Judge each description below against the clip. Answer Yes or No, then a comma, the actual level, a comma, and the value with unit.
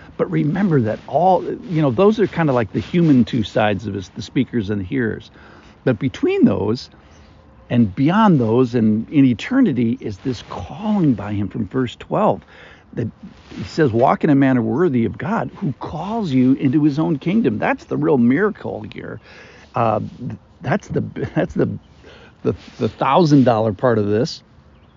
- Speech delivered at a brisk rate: No, average, 175 wpm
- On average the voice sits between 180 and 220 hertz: No, low, 130 Hz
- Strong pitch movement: Yes, wide, 6.9 semitones